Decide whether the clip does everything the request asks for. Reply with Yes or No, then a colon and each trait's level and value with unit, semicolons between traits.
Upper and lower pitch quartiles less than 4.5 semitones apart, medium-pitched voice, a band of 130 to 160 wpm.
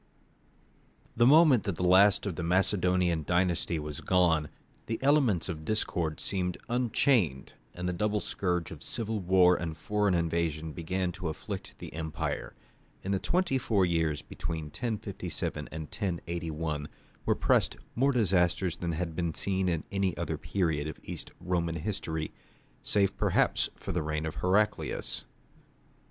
No: average, 3.6 semitones; very low, 90 Hz; average, 145 wpm